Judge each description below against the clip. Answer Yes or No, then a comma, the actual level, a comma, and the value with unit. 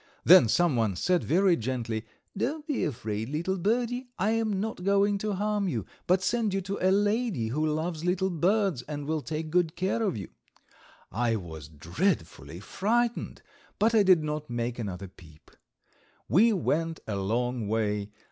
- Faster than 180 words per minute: No, average, 165 wpm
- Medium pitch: Yes, medium, 165 Hz